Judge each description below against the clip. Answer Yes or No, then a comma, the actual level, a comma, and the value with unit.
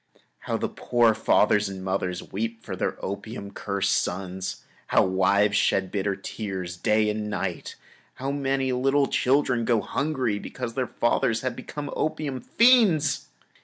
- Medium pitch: No, low, 110 Hz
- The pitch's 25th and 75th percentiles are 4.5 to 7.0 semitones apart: Yes, average, 5.1 semitones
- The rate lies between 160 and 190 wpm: No, average, 150 wpm